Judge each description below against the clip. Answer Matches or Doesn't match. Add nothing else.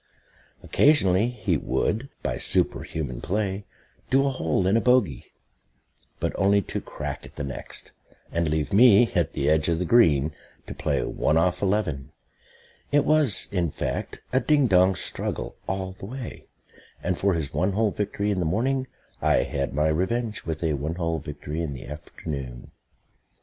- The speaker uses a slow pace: Doesn't match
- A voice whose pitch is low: Matches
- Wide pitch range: Matches